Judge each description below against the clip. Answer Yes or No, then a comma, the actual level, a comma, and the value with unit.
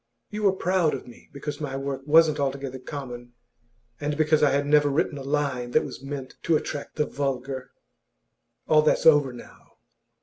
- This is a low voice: No, medium, 145 Hz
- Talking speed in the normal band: Yes, average, 175 wpm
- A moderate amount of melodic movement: No, narrow, 2.0 semitones